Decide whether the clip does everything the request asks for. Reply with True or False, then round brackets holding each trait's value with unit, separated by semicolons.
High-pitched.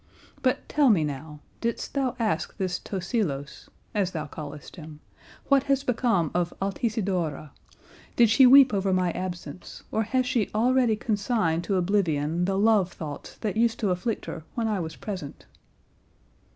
True (195 Hz)